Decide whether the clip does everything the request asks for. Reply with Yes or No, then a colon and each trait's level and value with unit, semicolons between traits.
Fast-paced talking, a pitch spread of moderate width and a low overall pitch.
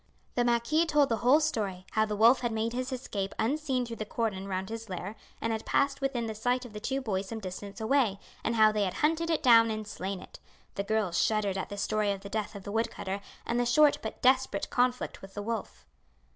No: fast, 240 wpm; average, 3.6 semitones; high, 225 Hz